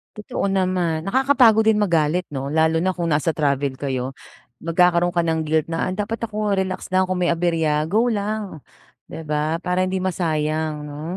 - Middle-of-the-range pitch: Yes, medium, 170 Hz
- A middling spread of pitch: Yes, average, 3.3 semitones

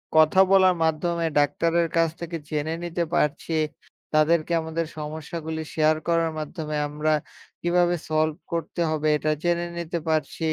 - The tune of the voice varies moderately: No, narrow, 1.6 semitones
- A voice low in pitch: No, medium, 160 Hz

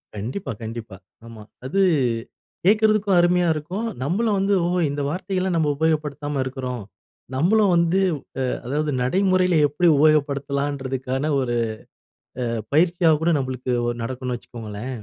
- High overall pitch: No, medium, 150 Hz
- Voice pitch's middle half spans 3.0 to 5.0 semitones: No, wide, 5.6 semitones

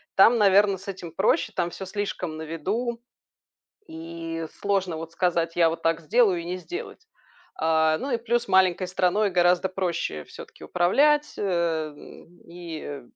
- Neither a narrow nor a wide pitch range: Yes, average, 3.4 semitones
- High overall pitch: No, medium, 180 Hz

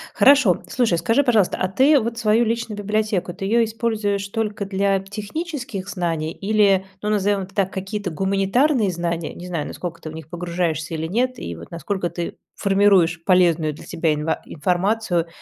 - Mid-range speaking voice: No, high, 195 Hz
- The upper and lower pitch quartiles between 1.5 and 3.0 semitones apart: No, average, 3.9 semitones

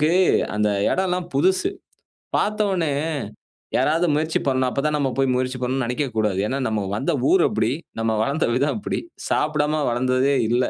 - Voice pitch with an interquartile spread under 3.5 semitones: No, average, 3.9 semitones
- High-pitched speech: No, medium, 140 Hz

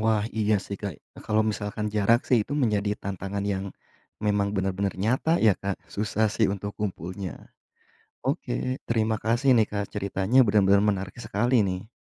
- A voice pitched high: No, low, 105 Hz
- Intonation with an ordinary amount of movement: No, narrow, 2.1 semitones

